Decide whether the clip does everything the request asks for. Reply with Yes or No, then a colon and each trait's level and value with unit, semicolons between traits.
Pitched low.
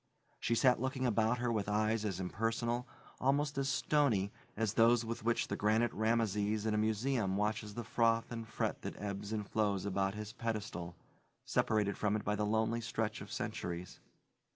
Yes: low, 110 Hz